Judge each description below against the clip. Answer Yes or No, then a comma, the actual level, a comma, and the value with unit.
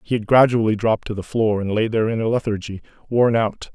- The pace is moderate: No, fast, 240 wpm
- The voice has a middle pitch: No, low, 110 Hz